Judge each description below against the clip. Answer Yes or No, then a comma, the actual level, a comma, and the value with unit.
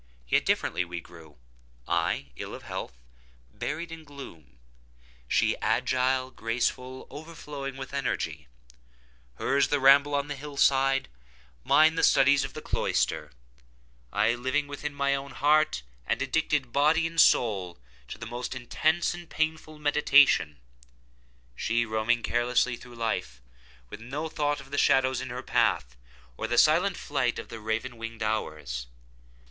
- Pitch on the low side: Yes, low, 125 Hz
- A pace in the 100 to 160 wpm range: Yes, average, 140 wpm